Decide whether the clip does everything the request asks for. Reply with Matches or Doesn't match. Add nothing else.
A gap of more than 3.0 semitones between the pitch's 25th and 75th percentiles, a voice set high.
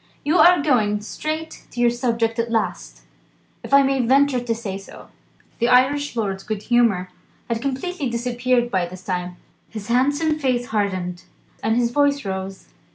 Matches